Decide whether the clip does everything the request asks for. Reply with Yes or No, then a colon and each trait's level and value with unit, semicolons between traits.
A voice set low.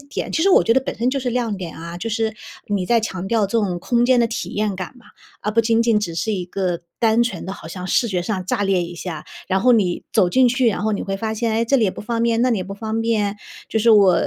No: high, 220 Hz